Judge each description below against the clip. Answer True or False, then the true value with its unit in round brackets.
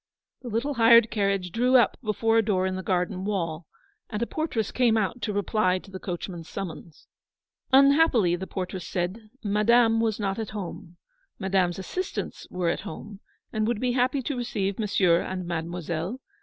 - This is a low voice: False (205 Hz)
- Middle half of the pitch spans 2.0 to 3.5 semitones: False (4.1 semitones)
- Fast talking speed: False (175 wpm)